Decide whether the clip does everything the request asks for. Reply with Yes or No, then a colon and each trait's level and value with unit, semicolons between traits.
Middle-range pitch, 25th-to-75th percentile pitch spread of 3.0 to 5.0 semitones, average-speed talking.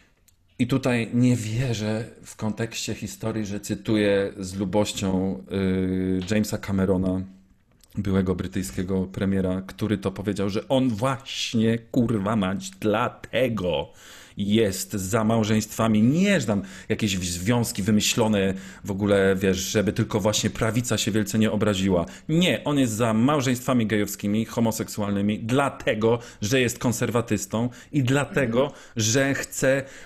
No: low, 110 Hz; average, 3.5 semitones; average, 120 wpm